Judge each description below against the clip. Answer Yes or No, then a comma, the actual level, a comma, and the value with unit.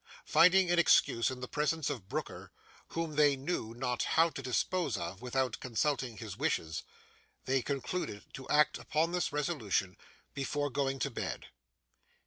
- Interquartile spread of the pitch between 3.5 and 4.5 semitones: Yes, average, 4.2 semitones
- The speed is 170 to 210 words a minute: No, average, 150 wpm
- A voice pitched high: No, low, 135 Hz